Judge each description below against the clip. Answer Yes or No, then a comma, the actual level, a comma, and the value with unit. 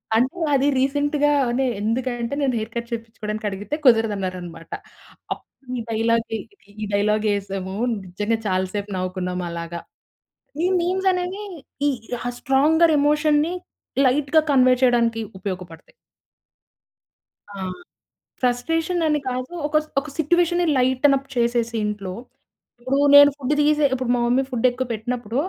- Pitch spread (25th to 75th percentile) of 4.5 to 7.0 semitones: Yes, wide, 5.4 semitones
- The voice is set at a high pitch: Yes, high, 245 Hz